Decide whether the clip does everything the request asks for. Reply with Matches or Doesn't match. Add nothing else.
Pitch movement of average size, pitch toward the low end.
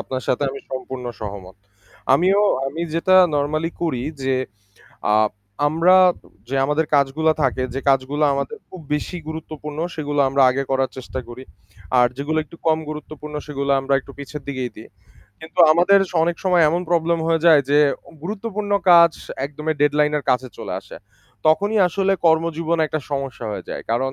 Doesn't match